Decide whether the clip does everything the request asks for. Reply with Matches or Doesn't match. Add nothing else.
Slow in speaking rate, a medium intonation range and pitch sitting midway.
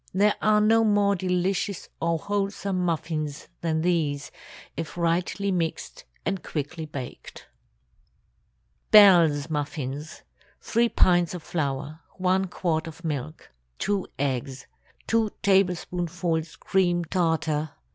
Matches